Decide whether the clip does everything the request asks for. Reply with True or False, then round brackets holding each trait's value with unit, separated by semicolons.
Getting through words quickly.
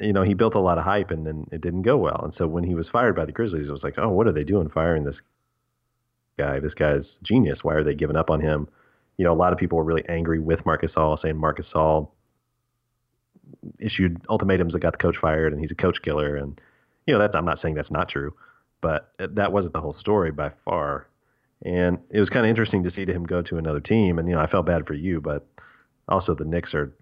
True (255 wpm)